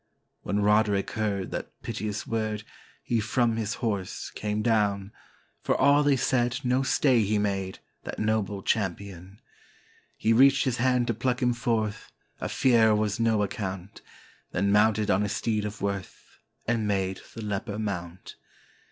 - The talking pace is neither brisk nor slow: Yes, average, 150 wpm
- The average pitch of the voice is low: Yes, low, 105 Hz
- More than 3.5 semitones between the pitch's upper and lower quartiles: No, narrow, 2.6 semitones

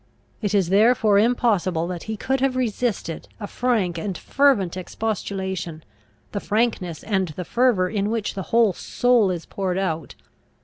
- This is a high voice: Yes, high, 200 Hz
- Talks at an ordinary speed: Yes, average, 150 wpm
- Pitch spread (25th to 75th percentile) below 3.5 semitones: No, average, 4.1 semitones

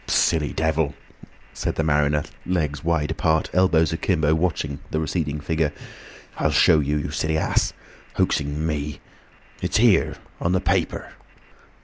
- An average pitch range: No, narrow, 1.6 semitones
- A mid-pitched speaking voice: No, very low, 80 Hz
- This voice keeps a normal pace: No, slow, 125 wpm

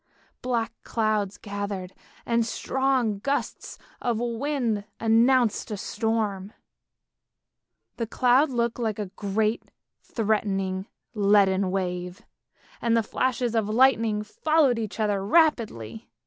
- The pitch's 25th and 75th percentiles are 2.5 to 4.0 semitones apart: Yes, average, 2.9 semitones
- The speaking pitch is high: Yes, high, 220 Hz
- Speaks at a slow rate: Yes, slow, 105 wpm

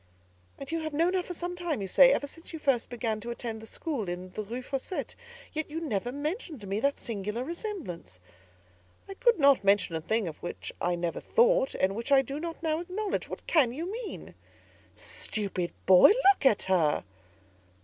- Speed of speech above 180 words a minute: Yes, average, 190 wpm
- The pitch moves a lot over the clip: Yes, wide, 8.6 semitones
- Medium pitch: No, very high, 275 Hz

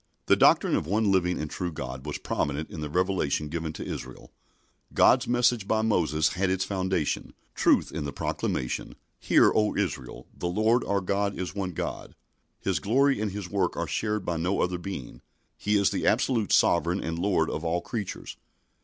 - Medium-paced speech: Yes, average, 185 wpm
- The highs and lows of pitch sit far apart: No, average, 4.1 semitones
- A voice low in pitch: Yes, very low, 95 Hz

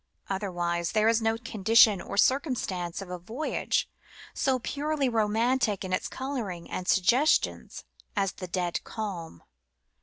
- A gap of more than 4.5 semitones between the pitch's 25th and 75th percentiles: Yes, average, 4.9 semitones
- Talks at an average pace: No, slow, 130 wpm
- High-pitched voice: Yes, high, 215 Hz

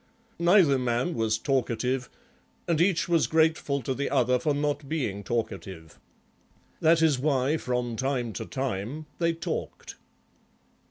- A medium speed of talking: No, slow, 130 wpm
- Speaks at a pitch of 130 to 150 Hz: Yes, low, 135 Hz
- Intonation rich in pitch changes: No, average, 4.7 semitones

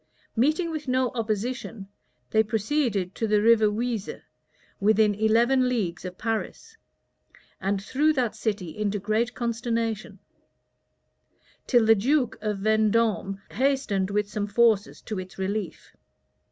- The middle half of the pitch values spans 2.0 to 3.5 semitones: Yes, average, 2.8 semitones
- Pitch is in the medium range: No, high, 220 Hz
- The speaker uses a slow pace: Yes, slow, 125 wpm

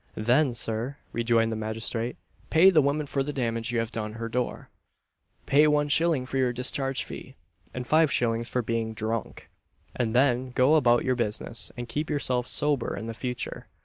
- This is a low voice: Yes, low, 125 Hz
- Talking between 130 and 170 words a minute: No, average, 180 wpm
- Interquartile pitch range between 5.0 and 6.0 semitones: No, average, 3.5 semitones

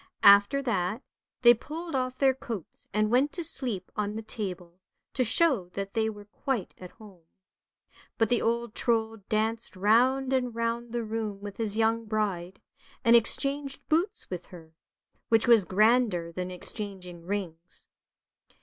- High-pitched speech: Yes, high, 220 Hz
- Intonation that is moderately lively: Yes, average, 3.6 semitones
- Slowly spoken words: No, average, 150 wpm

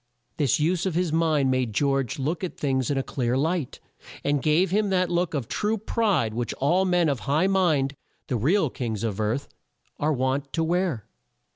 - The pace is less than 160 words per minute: No, average, 190 wpm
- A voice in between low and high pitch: Yes, medium, 150 Hz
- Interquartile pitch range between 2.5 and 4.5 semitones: No, average, 5.2 semitones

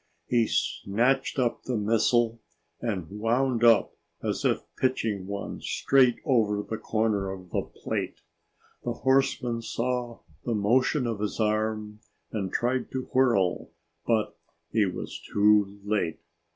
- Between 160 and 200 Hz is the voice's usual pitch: No, low, 115 Hz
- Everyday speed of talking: No, slow, 130 wpm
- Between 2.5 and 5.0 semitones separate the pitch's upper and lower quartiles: Yes, average, 2.9 semitones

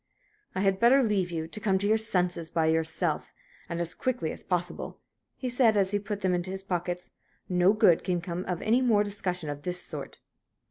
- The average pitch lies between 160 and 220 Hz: Yes, medium, 185 Hz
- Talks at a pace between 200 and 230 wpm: Yes, fast, 205 wpm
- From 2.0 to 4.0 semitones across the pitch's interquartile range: Yes, average, 3.1 semitones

